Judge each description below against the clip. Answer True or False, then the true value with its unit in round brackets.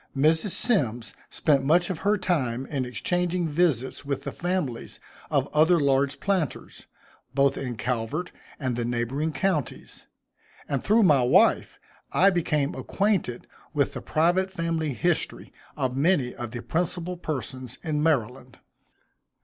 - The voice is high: False (150 Hz)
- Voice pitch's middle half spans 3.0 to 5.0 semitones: False (5.4 semitones)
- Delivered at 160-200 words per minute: False (140 wpm)